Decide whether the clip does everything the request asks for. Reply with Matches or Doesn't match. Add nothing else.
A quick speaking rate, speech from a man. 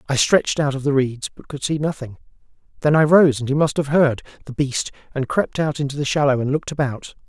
Matches